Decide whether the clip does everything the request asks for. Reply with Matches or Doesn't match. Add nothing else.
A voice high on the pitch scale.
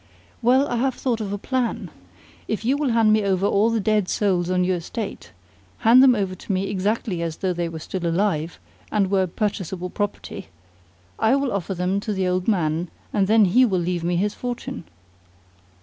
Matches